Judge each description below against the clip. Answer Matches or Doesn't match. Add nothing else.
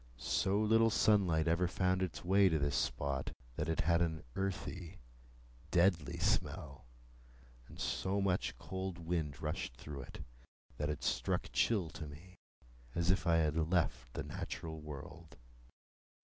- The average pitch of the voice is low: Matches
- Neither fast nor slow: Matches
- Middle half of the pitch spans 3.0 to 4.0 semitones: Matches